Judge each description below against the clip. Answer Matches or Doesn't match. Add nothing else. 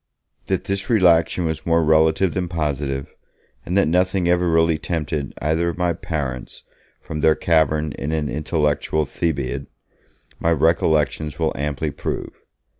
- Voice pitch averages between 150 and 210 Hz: Doesn't match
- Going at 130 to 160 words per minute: Matches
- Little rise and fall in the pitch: Matches